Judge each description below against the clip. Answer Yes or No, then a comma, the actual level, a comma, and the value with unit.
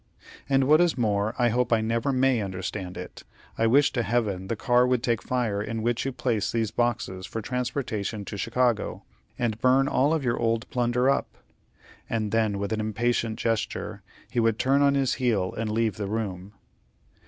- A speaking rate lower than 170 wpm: No, average, 190 wpm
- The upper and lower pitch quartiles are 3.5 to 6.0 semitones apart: No, average, 2.8 semitones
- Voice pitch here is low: Yes, low, 115 Hz